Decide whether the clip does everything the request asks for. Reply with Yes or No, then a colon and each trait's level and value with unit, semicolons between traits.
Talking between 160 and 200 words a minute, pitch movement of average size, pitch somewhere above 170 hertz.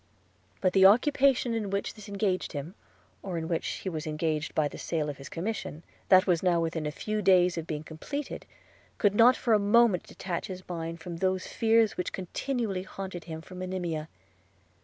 Yes: average, 190 wpm; average, 3.9 semitones; medium, 185 Hz